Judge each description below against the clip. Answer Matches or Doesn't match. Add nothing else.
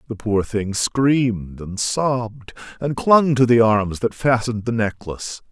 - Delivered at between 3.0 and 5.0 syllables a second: Matches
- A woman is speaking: Doesn't match